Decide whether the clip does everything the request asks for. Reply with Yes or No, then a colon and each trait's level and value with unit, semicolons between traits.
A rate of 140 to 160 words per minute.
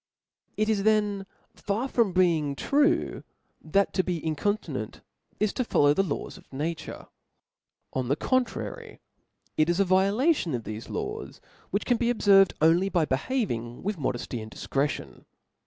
Yes: average, 150 wpm